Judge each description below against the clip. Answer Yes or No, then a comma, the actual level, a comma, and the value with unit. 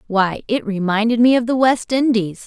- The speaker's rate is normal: Yes, average, 195 wpm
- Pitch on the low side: No, high, 225 Hz